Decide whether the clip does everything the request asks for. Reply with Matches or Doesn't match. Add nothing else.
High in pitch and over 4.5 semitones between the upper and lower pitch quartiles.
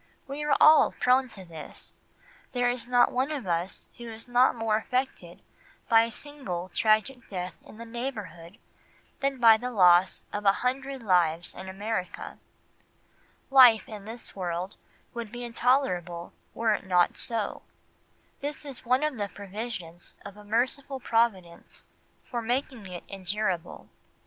Matches